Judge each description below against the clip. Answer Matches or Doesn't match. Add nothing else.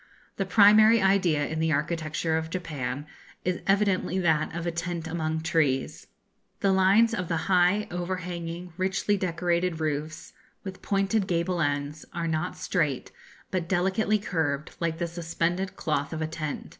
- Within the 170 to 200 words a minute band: Doesn't match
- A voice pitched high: Doesn't match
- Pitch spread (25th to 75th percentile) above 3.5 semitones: Doesn't match